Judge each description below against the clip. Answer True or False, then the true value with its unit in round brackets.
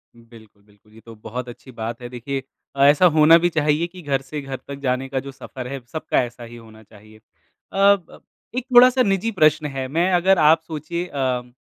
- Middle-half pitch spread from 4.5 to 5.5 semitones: True (5.2 semitones)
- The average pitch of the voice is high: False (135 Hz)